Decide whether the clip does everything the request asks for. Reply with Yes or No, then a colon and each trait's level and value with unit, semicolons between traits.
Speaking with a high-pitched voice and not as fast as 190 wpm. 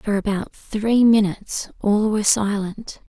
Yes: high, 210 Hz; slow, 135 wpm